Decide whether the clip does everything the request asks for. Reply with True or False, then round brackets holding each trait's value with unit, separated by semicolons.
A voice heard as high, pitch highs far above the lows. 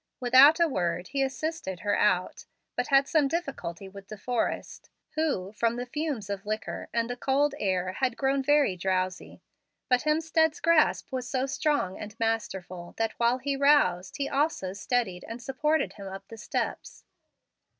True (245 Hz; 6.5 semitones)